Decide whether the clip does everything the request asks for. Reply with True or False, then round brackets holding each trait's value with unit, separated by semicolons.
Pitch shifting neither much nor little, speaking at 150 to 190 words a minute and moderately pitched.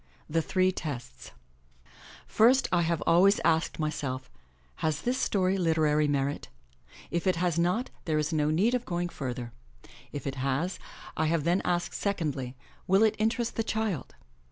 True (4.3 semitones; 155 wpm; 165 Hz)